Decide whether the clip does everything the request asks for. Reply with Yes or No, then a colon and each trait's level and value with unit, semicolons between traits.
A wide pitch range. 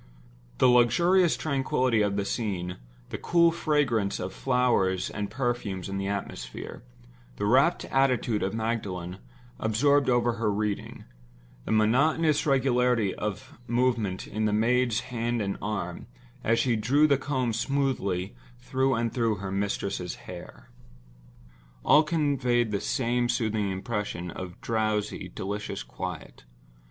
No: average, 4.4 semitones